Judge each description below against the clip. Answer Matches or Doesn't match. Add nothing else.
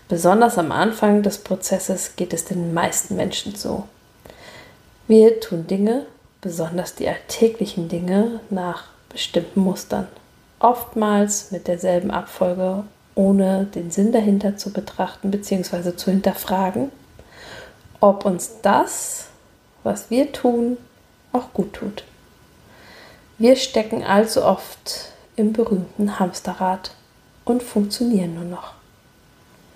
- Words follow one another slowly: Matches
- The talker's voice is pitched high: Matches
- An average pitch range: Matches